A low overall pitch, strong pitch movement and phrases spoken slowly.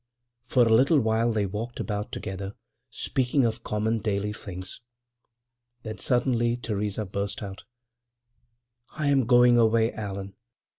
No: low, 110 Hz; average, 2.8 semitones; slow, 120 wpm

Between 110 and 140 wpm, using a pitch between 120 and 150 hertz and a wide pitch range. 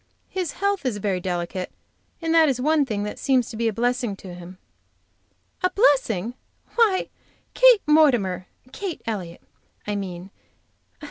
No: slow, 135 wpm; high, 235 Hz; wide, 8.7 semitones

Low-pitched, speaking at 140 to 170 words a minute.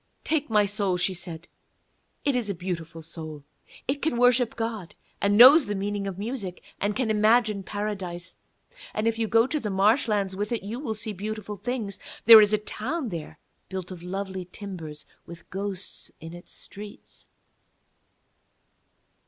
No: high, 205 Hz; average, 165 wpm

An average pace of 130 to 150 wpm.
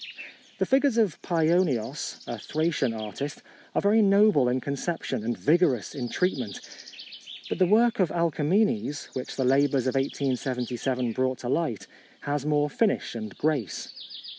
Yes: average, 140 wpm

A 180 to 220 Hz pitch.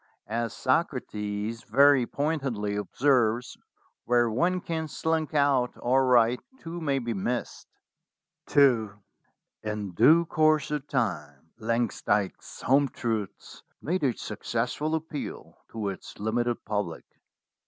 No: low, 120 Hz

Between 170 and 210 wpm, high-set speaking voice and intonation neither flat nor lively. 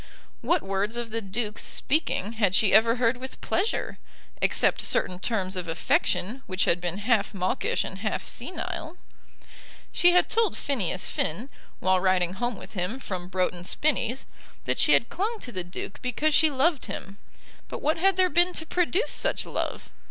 No: average, 175 wpm; high, 230 Hz; wide, 8.6 semitones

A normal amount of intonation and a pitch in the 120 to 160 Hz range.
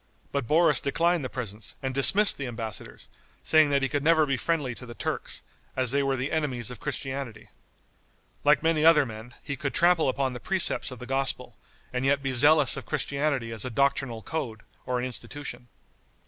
Yes: average, 3.3 semitones; low, 135 Hz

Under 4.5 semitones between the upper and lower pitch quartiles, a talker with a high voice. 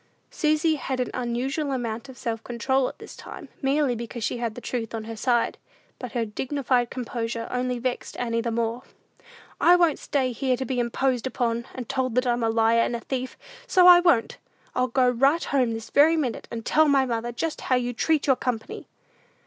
Yes: narrow, 2.5 semitones; very high, 250 Hz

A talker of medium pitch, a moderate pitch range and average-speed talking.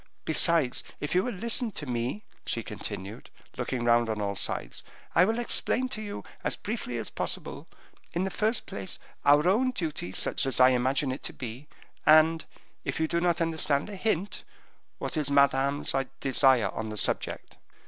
No: medium, 150 Hz; wide, 6.7 semitones; average, 175 wpm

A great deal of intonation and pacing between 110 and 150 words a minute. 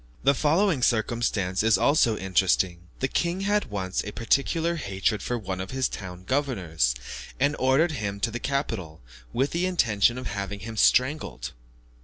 No: wide, 6.7 semitones; average, 160 wpm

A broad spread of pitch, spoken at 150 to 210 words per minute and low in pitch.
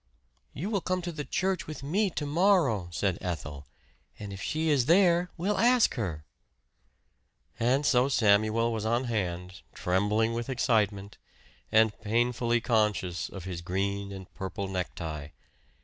No: wide, 7.5 semitones; average, 140 wpm; low, 110 Hz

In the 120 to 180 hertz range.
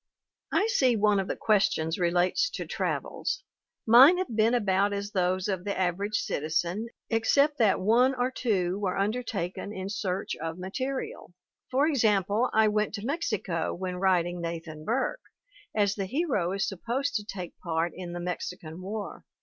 No: high, 200 Hz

